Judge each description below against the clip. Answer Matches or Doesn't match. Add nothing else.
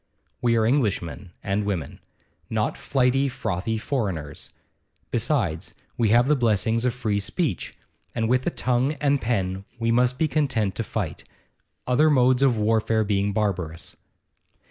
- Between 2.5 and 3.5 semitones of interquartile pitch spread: Doesn't match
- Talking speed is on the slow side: Doesn't match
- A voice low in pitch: Matches